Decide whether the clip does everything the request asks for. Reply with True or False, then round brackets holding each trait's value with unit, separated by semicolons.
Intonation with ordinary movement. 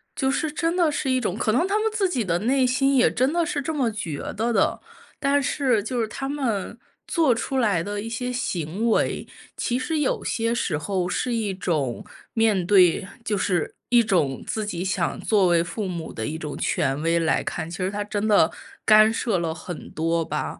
False (6.6 semitones)